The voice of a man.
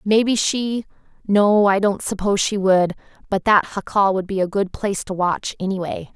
No: female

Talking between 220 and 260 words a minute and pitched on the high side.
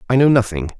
No: fast, 225 wpm; low, 115 Hz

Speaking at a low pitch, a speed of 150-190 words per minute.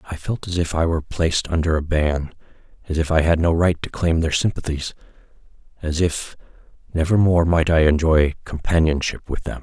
Yes: very low, 80 Hz; average, 175 wpm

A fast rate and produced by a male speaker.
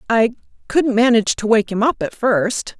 No: fast, 215 wpm; female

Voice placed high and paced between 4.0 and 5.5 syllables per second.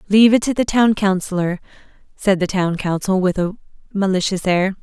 Yes: high, 195 Hz; 5.4 syllables/s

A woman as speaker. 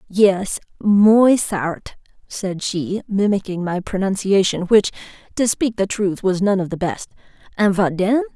Yes: female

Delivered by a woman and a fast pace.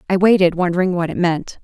Yes: female; fast, 220 wpm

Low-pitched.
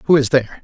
Yes: low, 130 Hz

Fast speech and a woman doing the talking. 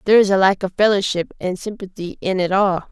Yes: fast, 225 wpm; female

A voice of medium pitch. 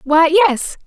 No: very high, 330 Hz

